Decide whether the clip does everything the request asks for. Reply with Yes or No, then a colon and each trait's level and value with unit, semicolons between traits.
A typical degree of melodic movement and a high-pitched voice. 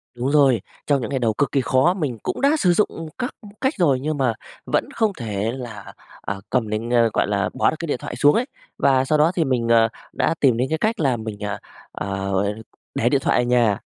No: average, 5.0 semitones; low, 130 Hz